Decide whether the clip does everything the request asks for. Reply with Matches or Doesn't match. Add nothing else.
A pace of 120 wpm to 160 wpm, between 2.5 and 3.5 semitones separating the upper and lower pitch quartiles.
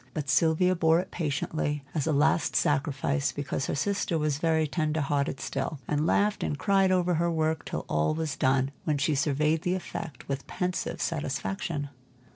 Doesn't match